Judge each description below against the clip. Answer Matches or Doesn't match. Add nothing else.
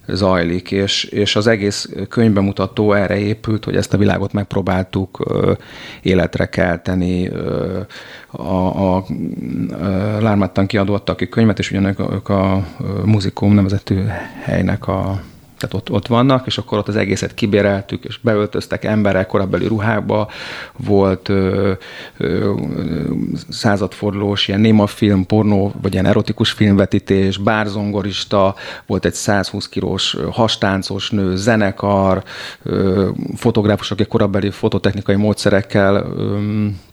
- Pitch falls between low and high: Doesn't match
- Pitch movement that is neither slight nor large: Doesn't match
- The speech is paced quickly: Doesn't match